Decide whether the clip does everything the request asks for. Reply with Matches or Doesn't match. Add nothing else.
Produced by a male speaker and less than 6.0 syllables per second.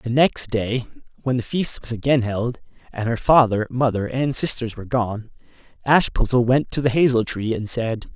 Matches